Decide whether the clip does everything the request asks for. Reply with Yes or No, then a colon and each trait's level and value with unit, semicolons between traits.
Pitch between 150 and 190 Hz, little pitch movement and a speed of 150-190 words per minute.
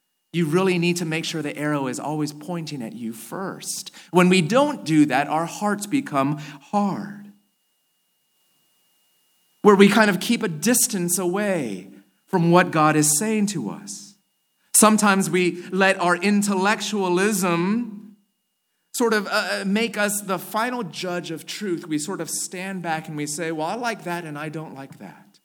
No: medium, 185 Hz; average, 4.2 semitones; average, 165 wpm